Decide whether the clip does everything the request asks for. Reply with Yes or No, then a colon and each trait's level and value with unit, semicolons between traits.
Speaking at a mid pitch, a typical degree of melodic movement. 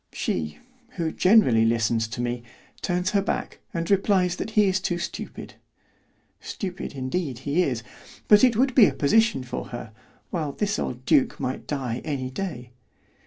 No: medium, 160 Hz; wide, 7.7 semitones